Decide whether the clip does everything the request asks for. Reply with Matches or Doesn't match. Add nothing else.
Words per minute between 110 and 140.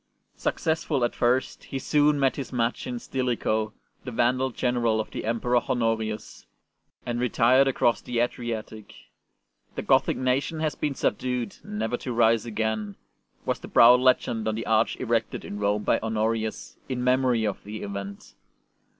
Doesn't match